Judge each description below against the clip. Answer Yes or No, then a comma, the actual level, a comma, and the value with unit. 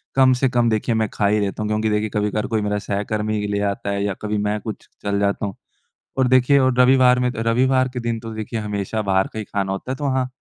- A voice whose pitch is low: Yes, low, 110 Hz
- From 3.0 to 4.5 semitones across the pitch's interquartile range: Yes, average, 3.3 semitones